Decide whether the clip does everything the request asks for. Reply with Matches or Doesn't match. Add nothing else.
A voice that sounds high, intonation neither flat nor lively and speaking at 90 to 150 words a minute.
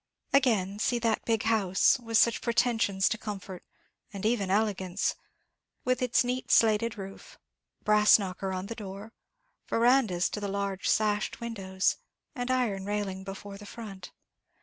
Matches